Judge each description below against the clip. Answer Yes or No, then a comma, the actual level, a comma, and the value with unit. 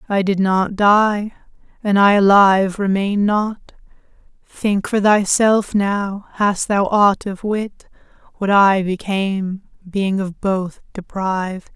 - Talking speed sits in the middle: No, slow, 130 wpm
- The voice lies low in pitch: No, high, 200 Hz